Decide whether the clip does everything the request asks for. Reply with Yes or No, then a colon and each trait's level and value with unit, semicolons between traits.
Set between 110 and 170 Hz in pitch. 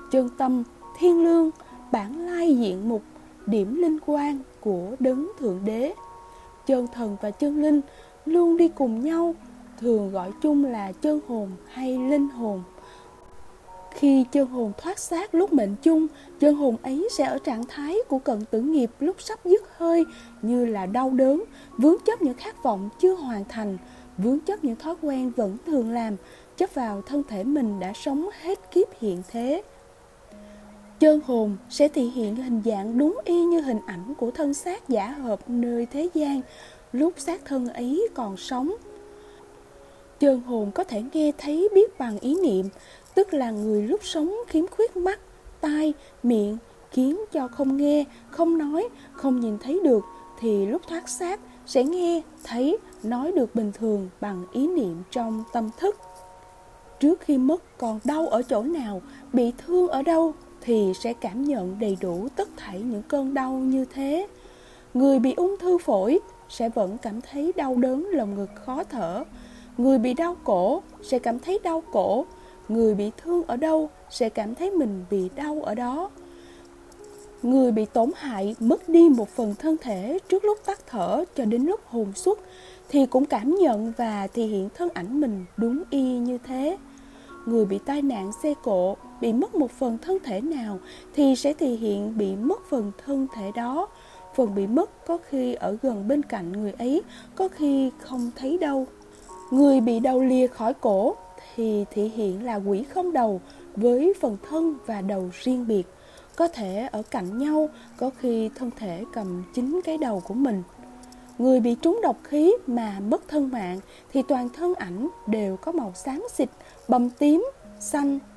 No: very high, 260 Hz